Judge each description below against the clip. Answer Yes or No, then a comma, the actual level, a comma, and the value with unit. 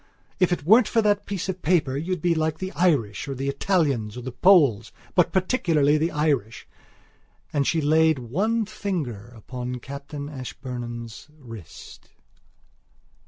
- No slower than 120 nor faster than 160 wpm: Yes, average, 145 wpm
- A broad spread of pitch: Yes, wide, 6.2 semitones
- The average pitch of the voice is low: No, medium, 150 Hz